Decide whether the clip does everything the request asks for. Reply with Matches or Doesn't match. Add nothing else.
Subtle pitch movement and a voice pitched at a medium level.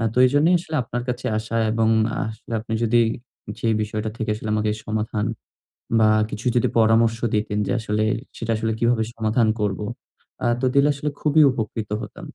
Doesn't match